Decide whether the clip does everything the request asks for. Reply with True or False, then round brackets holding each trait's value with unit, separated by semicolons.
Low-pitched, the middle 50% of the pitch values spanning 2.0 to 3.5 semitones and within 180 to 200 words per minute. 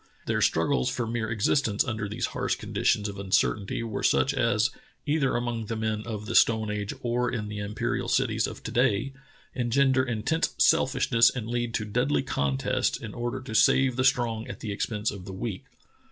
True (115 Hz; 2.8 semitones; 195 wpm)